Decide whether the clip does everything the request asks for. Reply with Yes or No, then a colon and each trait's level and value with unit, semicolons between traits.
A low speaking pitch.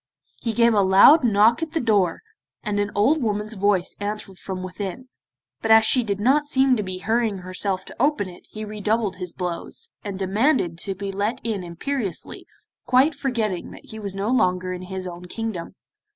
No: high, 205 Hz